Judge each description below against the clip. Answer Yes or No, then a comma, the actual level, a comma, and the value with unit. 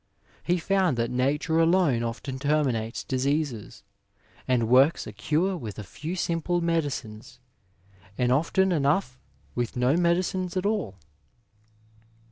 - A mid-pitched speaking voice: Yes, medium, 145 Hz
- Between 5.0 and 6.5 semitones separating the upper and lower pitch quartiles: Yes, wide, 5.6 semitones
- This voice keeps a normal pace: No, slow, 120 wpm